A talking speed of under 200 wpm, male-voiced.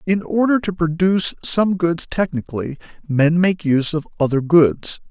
Yes: average, 155 wpm; male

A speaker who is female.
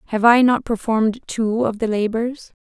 Yes: female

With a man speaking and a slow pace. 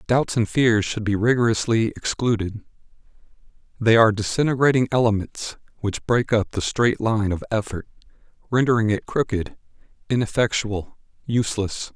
Yes: male; slow, 120 wpm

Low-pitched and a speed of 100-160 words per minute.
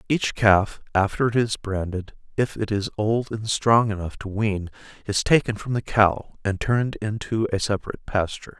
No: low, 105 Hz; average, 180 wpm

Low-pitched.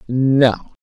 Yes: low, 130 Hz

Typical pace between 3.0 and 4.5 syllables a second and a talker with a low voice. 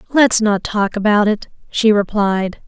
No: 4.0 syllables/s; high, 210 Hz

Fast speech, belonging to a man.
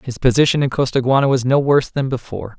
Yes: fast, 210 wpm; male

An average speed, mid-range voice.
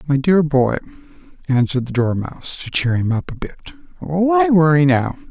Yes: average, 170 wpm; medium, 155 Hz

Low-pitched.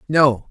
No: medium, 155 Hz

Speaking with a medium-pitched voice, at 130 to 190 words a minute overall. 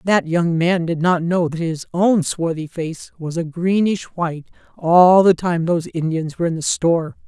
No: medium, 170 Hz; average, 200 wpm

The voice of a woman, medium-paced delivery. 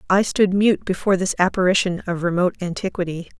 Yes: female; average, 160 wpm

